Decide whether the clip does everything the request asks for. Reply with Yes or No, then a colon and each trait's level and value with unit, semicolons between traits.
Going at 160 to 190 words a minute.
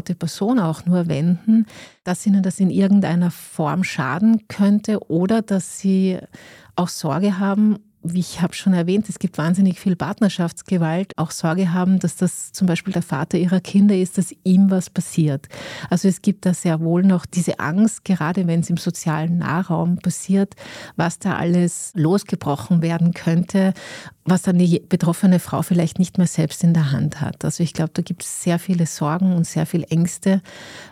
Yes: average, 180 wpm